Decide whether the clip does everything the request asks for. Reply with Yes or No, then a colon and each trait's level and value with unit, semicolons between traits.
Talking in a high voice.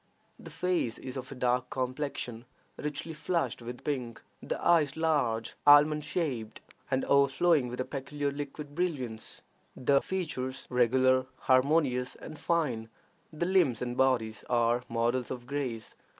No: low, 130 Hz